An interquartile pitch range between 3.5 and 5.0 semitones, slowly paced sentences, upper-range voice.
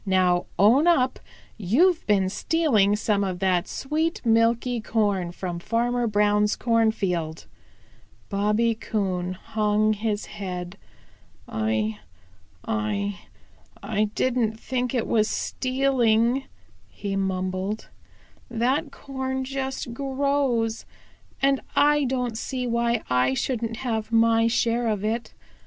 Yes: average, 3.9 semitones; slow, 110 wpm; high, 225 Hz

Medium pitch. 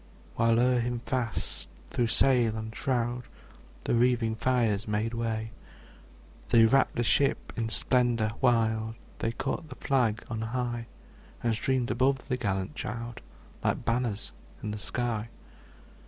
No: low, 115 Hz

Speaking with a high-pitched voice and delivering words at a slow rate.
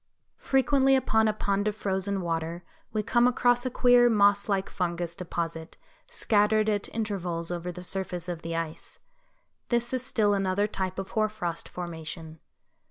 No: high, 195 Hz; average, 160 wpm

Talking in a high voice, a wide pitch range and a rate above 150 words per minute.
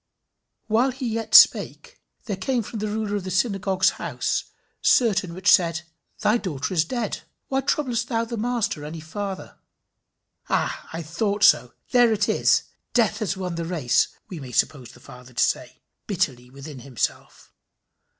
Yes: high, 195 Hz; wide, 6.0 semitones; average, 160 wpm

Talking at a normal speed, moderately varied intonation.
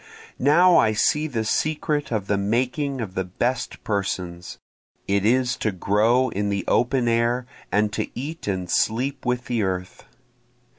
Yes: average, 155 wpm; average, 4.4 semitones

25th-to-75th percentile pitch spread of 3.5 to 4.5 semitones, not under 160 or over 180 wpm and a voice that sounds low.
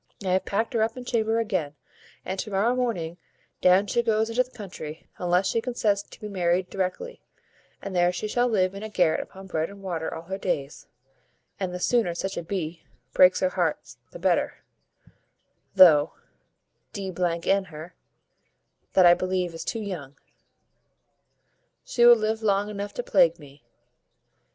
No: average, 3.8 semitones; average, 170 wpm; high, 190 Hz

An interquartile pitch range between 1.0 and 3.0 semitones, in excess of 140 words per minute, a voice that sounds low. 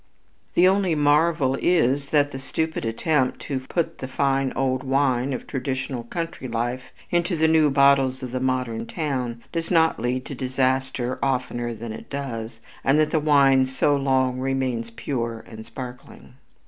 Yes: narrow, 2.5 semitones; average, 160 wpm; low, 130 Hz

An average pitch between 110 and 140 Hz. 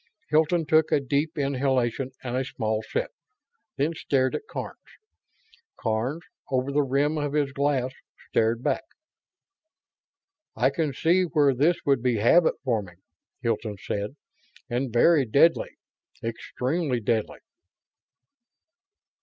Yes: low, 135 Hz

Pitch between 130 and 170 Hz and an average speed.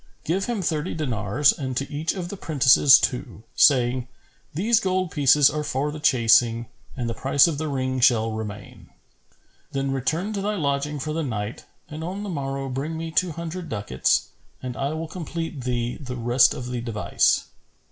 Yes: medium, 140 Hz; average, 180 wpm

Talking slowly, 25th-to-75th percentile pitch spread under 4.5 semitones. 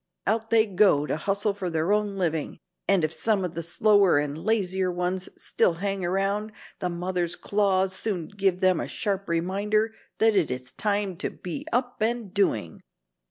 No: average, 175 wpm; average, 3.0 semitones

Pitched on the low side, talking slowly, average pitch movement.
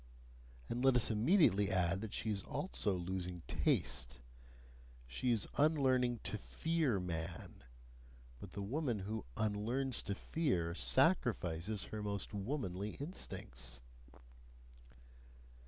No: low, 105 Hz; slow, 110 wpm; wide, 6.1 semitones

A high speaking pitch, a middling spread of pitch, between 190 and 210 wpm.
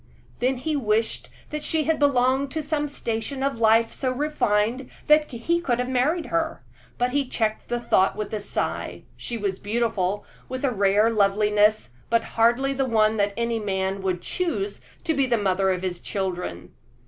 No: high, 235 Hz; average, 4.8 semitones; average, 180 wpm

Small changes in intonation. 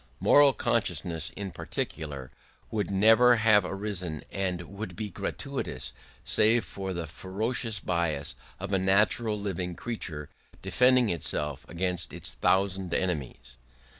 No: average, 3.8 semitones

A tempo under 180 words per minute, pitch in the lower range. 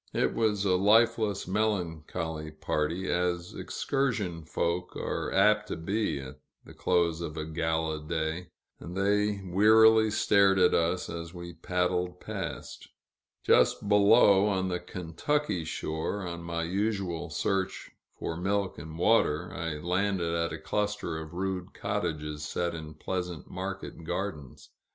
Yes: slow, 135 wpm; very low, 90 Hz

